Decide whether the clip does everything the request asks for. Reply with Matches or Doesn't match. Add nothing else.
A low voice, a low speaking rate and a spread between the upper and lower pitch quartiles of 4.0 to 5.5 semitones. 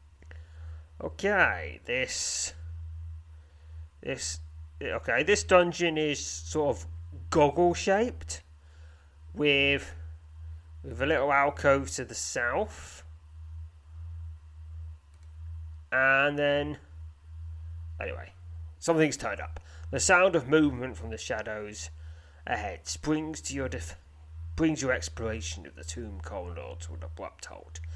Matches